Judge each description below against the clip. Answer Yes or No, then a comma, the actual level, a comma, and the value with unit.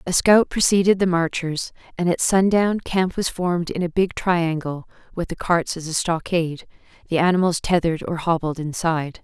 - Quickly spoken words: No, average, 175 wpm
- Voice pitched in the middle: Yes, medium, 175 Hz